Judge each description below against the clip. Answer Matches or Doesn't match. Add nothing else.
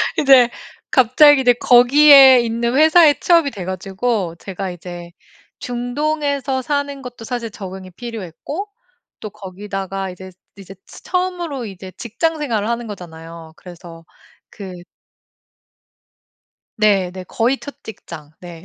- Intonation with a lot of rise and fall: Matches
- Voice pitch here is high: Matches